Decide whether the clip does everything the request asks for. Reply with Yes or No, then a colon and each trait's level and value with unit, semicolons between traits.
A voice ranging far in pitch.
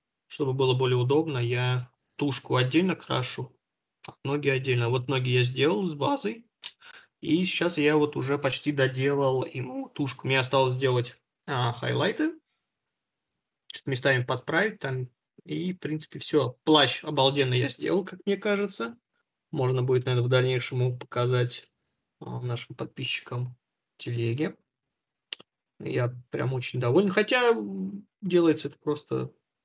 No: average, 4.0 semitones